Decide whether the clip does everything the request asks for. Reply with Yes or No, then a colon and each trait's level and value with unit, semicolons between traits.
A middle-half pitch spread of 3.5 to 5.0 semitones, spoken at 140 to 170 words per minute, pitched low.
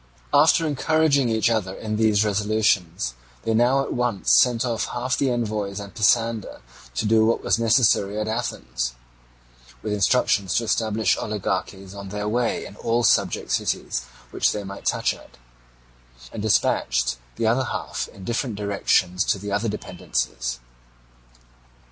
No: average, 3.0 semitones; average, 150 wpm; low, 110 Hz